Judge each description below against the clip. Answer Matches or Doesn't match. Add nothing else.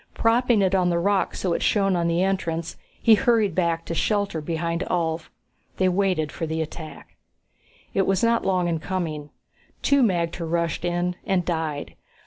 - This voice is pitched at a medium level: Matches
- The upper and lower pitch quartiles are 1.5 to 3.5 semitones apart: Matches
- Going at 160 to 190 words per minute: Matches